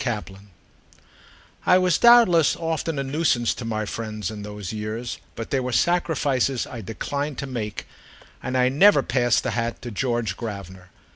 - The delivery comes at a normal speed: Yes, average, 160 wpm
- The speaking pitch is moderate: No, low, 120 Hz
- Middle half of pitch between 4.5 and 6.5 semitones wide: Yes, average, 4.8 semitones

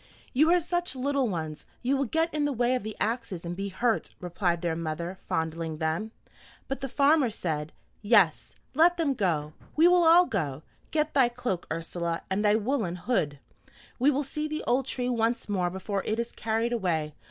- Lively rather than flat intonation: Yes, wide, 8.0 semitones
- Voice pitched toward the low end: No, high, 225 Hz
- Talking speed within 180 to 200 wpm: Yes, average, 190 wpm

